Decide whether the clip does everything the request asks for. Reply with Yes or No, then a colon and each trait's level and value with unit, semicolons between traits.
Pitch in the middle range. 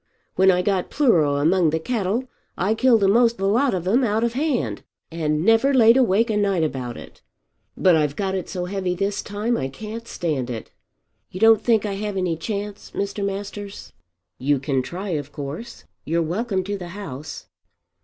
No: high, 195 Hz